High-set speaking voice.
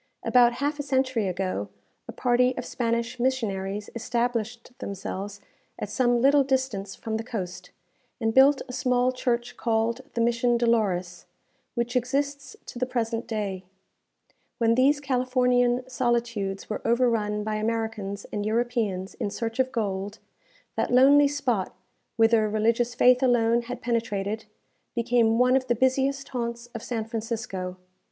Yes: high, 235 Hz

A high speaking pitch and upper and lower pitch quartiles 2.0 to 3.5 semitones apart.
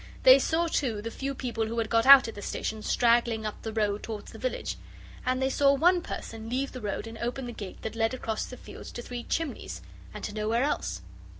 Yes: high, 235 Hz; average, 3.2 semitones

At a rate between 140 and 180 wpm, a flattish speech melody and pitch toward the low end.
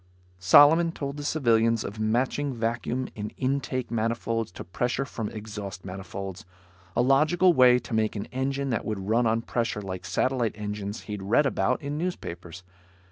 No: average, 160 wpm; average, 4.4 semitones; low, 115 Hz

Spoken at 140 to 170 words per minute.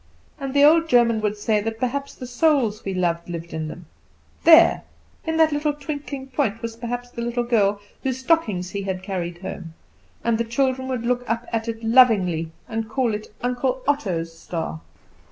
No: average, 185 wpm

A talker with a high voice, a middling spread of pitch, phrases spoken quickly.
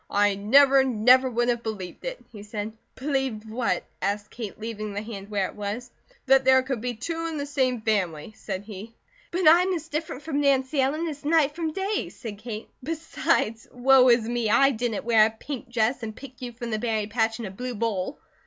Yes: high, 240 Hz; average, 4.1 semitones; fast, 210 wpm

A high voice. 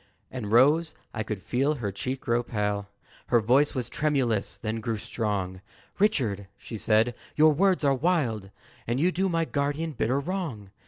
No: low, 125 Hz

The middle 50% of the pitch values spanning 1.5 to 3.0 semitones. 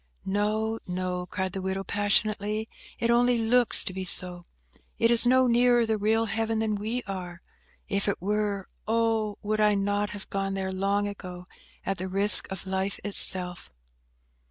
Yes: average, 2.7 semitones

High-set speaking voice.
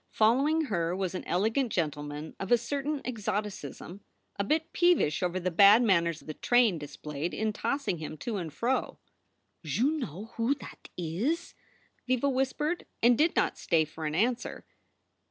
Yes: high, 210 Hz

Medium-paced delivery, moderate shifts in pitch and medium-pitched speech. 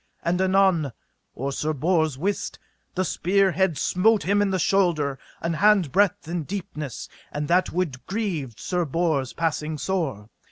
Yes: average, 155 wpm; average, 4.2 semitones; medium, 170 Hz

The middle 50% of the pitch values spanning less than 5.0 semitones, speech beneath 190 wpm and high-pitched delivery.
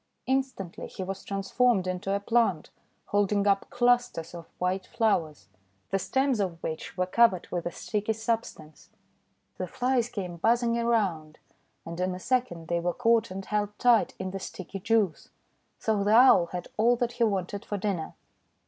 Yes: average, 4.3 semitones; average, 165 wpm; high, 200 Hz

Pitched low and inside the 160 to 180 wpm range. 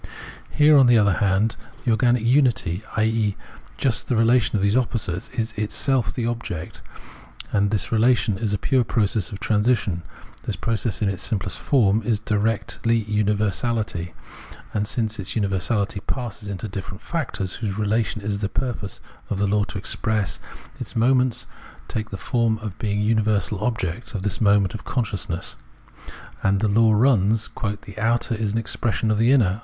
Yes: low, 110 Hz; average, 165 wpm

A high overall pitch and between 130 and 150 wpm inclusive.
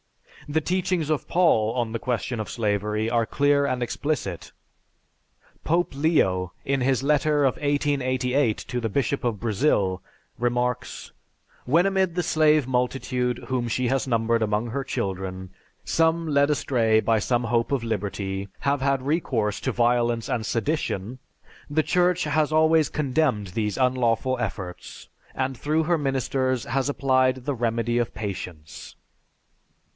No: low, 125 Hz; average, 140 wpm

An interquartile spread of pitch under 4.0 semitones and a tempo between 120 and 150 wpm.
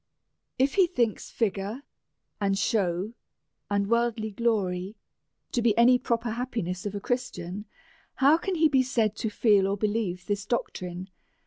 Yes: average, 3.6 semitones; average, 145 wpm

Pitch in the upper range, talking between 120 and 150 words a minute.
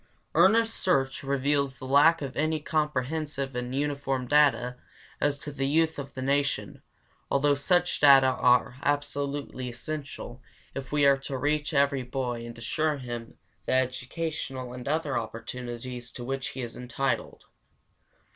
No: low, 135 Hz; average, 145 wpm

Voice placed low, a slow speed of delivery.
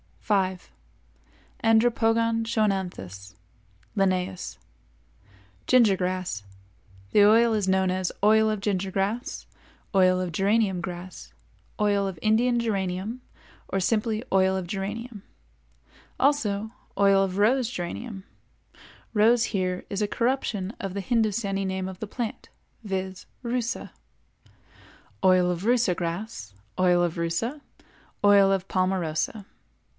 No: high, 195 Hz; slow, 110 wpm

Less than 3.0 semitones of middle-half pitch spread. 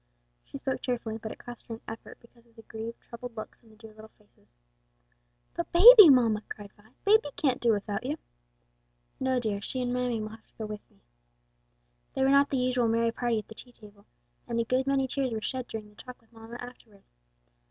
Yes: narrow, 2.6 semitones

